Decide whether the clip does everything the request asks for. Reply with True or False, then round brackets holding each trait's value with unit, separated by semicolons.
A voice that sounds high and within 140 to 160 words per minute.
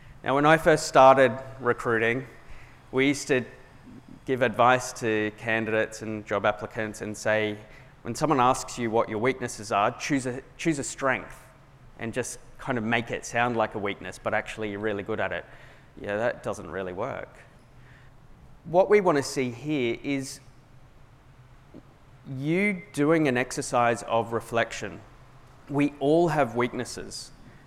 False (125 Hz; 150 wpm)